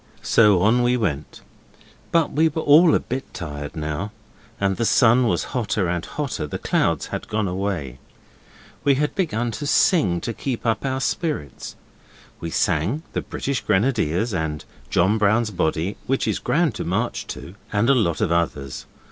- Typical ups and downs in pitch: No, wide, 7.4 semitones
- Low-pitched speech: Yes, low, 105 Hz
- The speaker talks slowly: No, average, 175 wpm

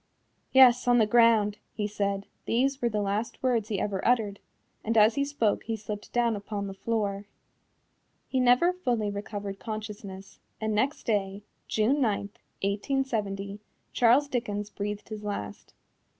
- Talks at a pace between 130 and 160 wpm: Yes, average, 150 wpm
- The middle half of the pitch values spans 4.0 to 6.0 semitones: No, average, 3.0 semitones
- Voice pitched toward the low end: No, high, 215 Hz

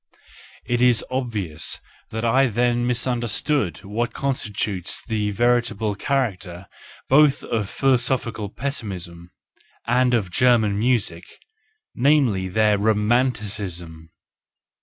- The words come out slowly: Yes, slow, 100 wpm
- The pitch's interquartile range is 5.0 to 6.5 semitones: No, average, 3.9 semitones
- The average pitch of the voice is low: Yes, low, 115 Hz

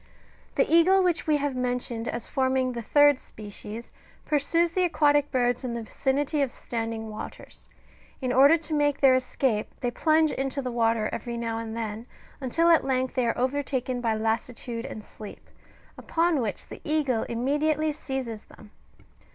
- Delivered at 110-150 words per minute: No, average, 165 wpm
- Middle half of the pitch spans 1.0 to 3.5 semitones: No, average, 4.0 semitones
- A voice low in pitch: No, very high, 255 Hz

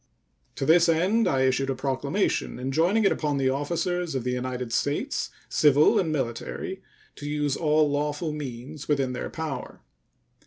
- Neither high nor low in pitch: Yes, medium, 145 Hz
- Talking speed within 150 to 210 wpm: Yes, average, 155 wpm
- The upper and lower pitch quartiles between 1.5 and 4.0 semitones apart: Yes, average, 3.3 semitones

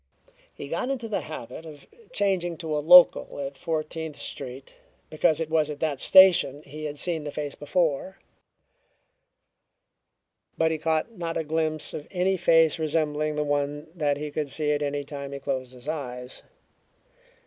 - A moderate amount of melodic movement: No, narrow, 2.1 semitones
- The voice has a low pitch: No, medium, 155 Hz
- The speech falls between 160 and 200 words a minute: Yes, average, 165 wpm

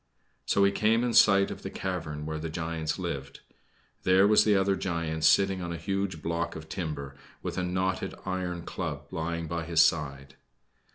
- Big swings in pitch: No, average, 3.3 semitones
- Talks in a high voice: No, very low, 85 Hz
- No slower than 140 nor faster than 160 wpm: No, average, 180 wpm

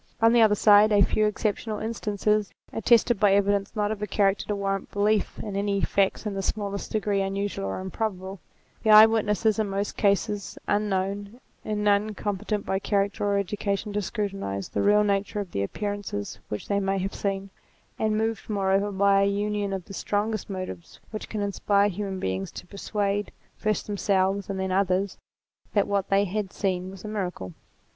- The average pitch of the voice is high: Yes, high, 200 Hz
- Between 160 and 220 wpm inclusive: Yes, average, 180 wpm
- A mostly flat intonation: Yes, narrow, 1.4 semitones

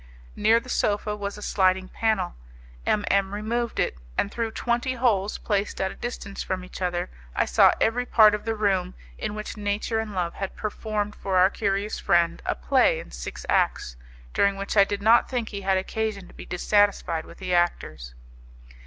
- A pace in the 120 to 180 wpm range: No, average, 190 wpm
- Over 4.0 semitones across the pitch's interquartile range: No, narrow, 2.6 semitones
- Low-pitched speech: No, high, 205 Hz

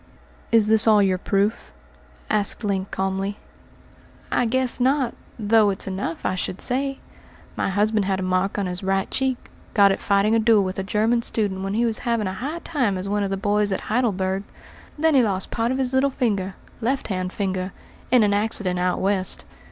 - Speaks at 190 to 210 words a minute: Yes, average, 200 wpm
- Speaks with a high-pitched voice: Yes, high, 205 Hz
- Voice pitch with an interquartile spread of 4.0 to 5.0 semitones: No, average, 3.4 semitones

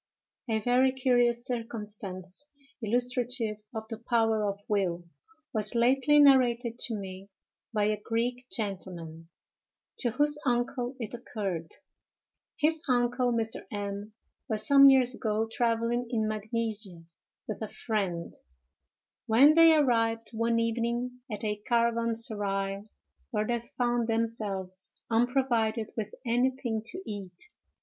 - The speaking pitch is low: No, high, 230 Hz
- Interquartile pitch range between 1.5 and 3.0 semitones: Yes, average, 2.7 semitones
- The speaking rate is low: Yes, slow, 120 wpm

